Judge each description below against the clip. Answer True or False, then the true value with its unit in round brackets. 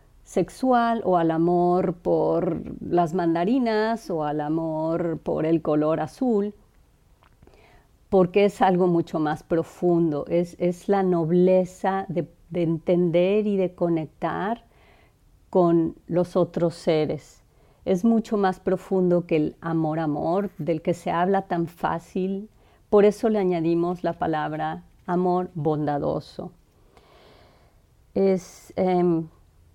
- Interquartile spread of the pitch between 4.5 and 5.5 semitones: False (2.5 semitones)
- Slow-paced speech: True (115 wpm)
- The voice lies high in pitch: False (175 Hz)